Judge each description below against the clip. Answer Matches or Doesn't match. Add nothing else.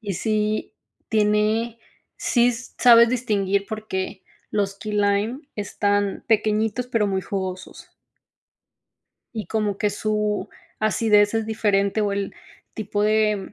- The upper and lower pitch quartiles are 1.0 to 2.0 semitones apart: Matches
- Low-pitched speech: Doesn't match